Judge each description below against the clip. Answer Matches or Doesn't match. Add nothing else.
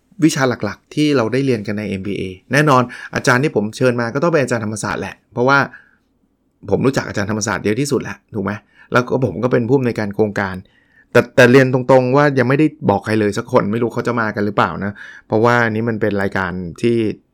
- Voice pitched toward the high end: Doesn't match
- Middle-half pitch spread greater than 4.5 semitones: Doesn't match